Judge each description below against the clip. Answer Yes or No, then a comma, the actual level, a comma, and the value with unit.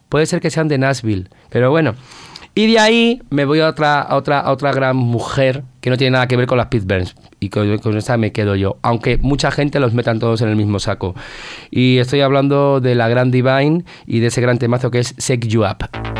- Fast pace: Yes, fast, 240 wpm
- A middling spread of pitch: Yes, average, 3.4 semitones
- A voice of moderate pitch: No, low, 125 Hz